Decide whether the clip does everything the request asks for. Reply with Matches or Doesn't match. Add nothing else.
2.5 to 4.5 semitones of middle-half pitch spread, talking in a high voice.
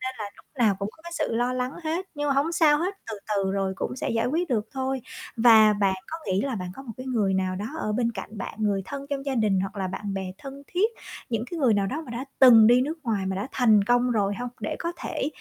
Doesn't match